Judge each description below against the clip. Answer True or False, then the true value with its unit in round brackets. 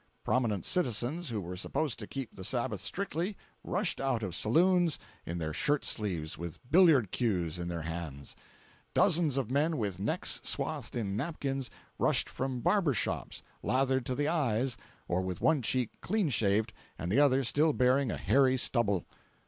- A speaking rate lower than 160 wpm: False (165 wpm)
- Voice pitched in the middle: False (125 Hz)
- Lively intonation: True (6.6 semitones)